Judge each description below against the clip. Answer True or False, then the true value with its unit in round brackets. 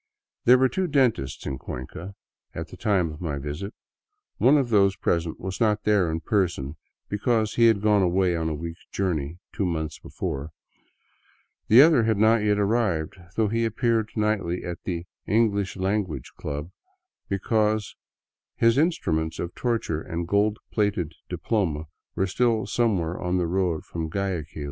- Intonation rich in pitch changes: False (4.7 semitones)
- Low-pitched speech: True (95 Hz)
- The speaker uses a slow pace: False (165 wpm)